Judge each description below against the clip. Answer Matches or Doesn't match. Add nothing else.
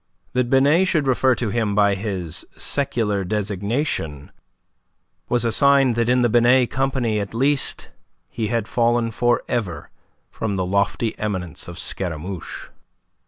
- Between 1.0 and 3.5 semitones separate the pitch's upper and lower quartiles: Doesn't match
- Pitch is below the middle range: Matches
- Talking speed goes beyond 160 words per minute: Doesn't match